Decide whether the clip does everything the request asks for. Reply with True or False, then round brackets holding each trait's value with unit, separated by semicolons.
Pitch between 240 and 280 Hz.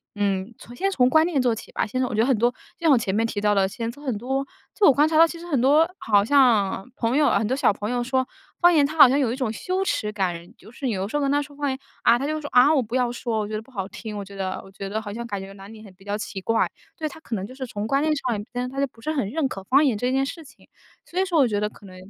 True (245 Hz)